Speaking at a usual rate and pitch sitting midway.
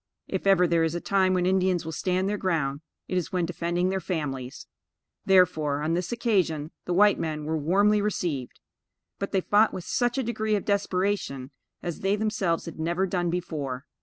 Yes: average, 190 wpm; medium, 180 Hz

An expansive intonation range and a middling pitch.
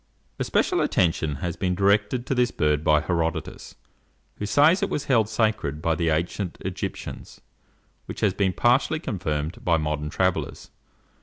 No: wide, 5.7 semitones; very low, 90 Hz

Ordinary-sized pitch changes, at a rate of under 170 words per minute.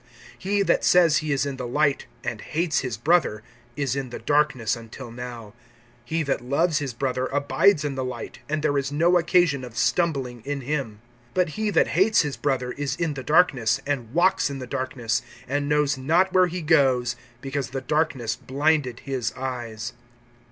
No: average, 3.8 semitones; average, 185 wpm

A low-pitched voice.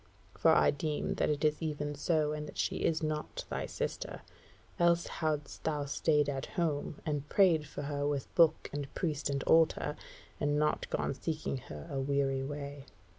No: medium, 150 Hz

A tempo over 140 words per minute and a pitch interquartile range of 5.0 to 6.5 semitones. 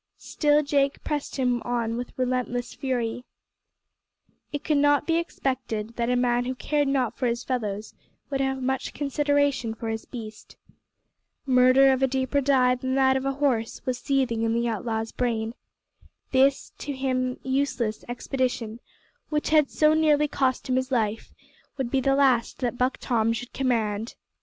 No: average, 165 wpm; narrow, 2.5 semitones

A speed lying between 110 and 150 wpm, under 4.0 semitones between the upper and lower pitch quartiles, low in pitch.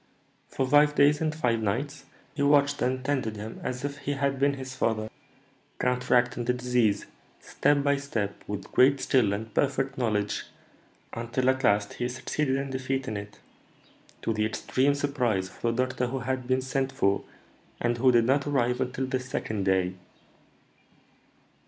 No: average, 165 wpm; average, 3.3 semitones; low, 130 Hz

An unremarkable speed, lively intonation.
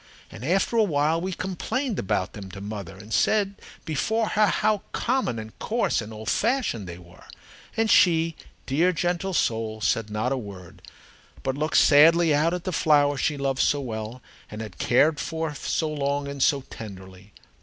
Yes: average, 175 wpm; wide, 8.1 semitones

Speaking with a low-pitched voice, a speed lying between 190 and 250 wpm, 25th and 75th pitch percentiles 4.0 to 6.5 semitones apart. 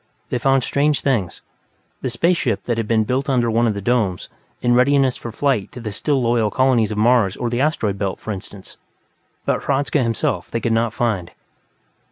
No: low, 120 Hz; average, 200 wpm; average, 3.5 semitones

